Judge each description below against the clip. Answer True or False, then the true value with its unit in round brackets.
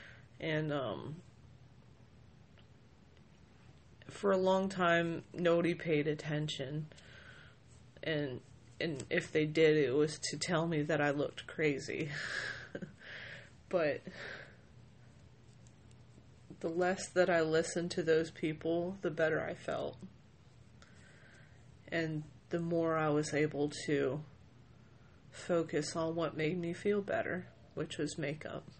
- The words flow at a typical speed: False (110 wpm)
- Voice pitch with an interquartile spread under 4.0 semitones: True (2.9 semitones)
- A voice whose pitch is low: False (155 Hz)